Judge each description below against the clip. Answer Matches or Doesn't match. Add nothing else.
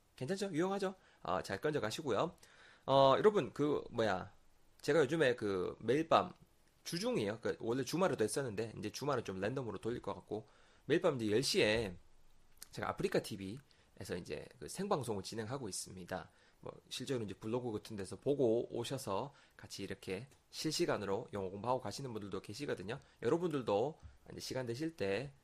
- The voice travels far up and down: Matches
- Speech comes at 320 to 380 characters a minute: Matches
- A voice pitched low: Matches